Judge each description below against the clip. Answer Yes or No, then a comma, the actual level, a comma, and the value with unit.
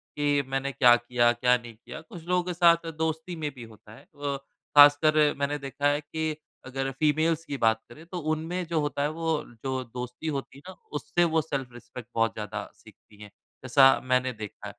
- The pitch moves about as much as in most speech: Yes, average, 4.2 semitones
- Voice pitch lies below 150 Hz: Yes, medium, 140 Hz